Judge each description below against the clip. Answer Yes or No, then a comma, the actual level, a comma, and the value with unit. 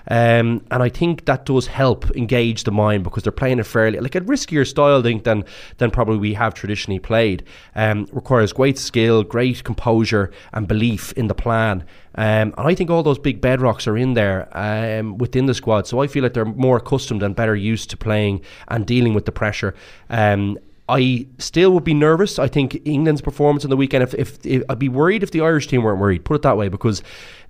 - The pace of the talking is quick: Yes, fast, 220 wpm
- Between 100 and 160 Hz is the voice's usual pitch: Yes, low, 115 Hz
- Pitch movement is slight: No, average, 4.0 semitones